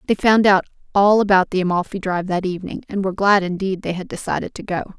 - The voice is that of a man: No, female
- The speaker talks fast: Yes, fast, 230 wpm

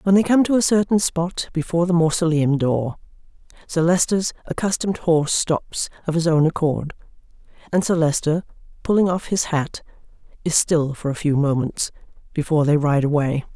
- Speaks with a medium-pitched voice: Yes, medium, 165 Hz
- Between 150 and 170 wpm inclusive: Yes, average, 165 wpm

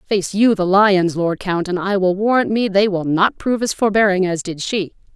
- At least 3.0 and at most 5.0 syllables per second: Yes, 4.9 syllables/s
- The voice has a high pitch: Yes, high, 195 Hz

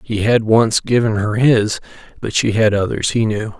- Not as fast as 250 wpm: Yes, average, 200 wpm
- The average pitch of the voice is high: No, low, 110 Hz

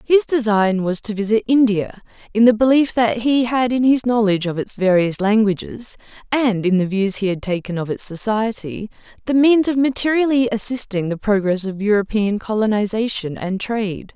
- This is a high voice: Yes, high, 220 Hz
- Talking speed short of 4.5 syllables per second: No, 5.1 syllables/s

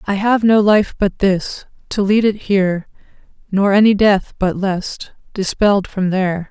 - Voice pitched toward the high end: Yes, high, 200 Hz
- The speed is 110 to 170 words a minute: Yes, average, 165 wpm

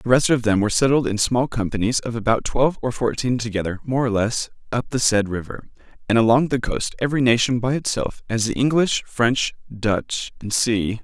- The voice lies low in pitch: Yes, low, 120 Hz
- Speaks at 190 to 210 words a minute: Yes, average, 200 wpm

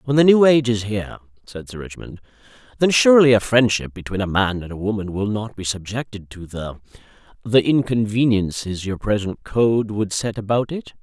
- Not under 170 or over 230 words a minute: Yes, average, 180 wpm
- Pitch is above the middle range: No, low, 110 Hz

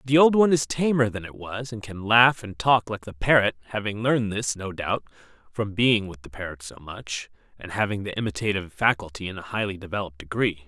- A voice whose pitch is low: Yes, low, 105 Hz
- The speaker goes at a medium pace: No, fast, 215 wpm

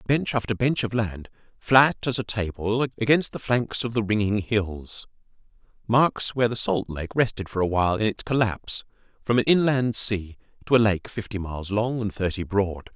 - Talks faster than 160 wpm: Yes, average, 185 wpm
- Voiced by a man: Yes, male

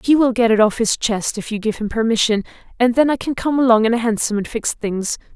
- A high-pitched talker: Yes, high, 230 Hz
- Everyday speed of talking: No, fast, 270 wpm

